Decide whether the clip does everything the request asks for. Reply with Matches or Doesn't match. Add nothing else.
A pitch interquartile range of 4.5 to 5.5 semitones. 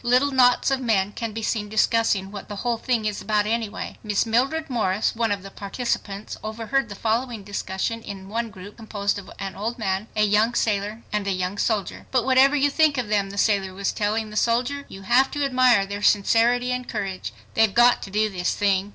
Doesn't match